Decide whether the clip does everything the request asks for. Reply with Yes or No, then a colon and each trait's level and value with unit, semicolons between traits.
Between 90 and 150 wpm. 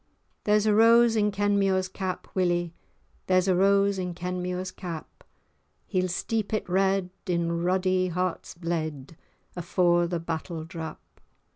Yes: average, 140 wpm